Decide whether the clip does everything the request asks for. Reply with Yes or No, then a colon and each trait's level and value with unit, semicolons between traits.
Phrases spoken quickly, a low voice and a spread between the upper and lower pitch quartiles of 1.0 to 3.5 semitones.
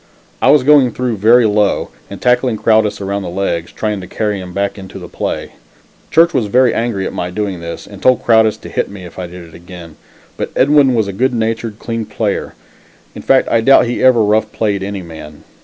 No: fast, 225 wpm; low, 105 Hz; average, 4.1 semitones